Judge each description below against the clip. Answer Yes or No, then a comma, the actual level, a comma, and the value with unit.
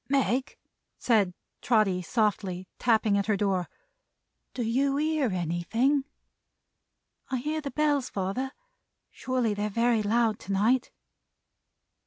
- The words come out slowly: Yes, slow, 115 wpm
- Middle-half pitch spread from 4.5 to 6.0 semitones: Yes, average, 4.8 semitones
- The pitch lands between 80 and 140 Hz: No, high, 230 Hz